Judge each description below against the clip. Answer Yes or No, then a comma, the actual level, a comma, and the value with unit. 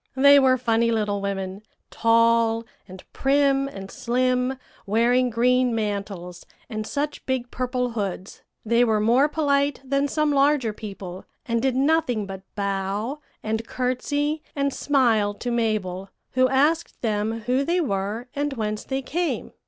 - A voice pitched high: Yes, high, 240 Hz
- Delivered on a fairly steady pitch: No, average, 4.4 semitones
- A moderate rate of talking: Yes, average, 145 wpm